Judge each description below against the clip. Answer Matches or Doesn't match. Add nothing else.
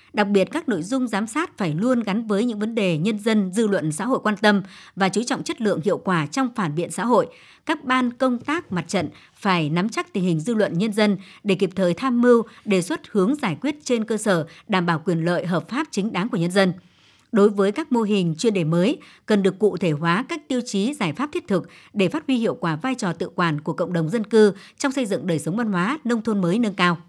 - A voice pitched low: Doesn't match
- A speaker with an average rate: Doesn't match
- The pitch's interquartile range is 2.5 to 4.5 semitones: Doesn't match